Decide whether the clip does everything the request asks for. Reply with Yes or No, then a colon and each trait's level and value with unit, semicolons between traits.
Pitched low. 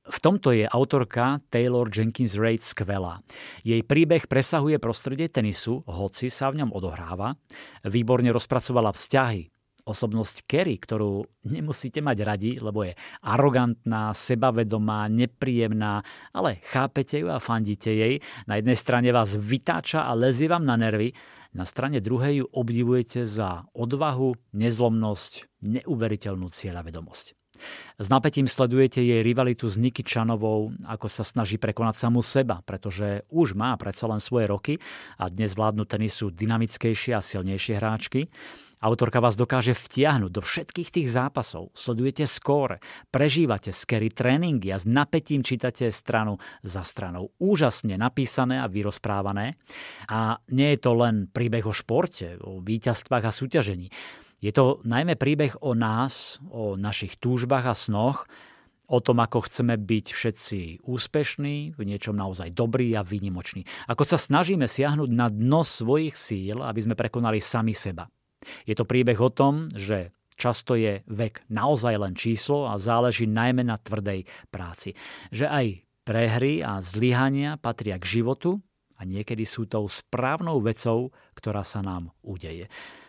Yes: low, 115 Hz